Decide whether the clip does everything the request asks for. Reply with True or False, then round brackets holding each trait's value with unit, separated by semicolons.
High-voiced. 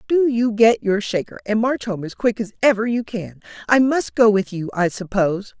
True (215 Hz)